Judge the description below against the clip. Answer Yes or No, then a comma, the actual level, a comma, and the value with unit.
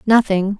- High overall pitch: Yes, high, 205 Hz